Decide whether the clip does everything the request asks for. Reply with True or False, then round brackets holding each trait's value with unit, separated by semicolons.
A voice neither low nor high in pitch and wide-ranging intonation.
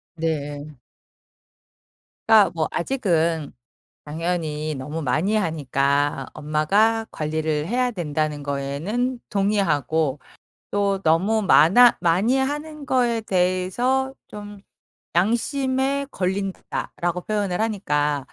True (180 Hz; 6.4 semitones)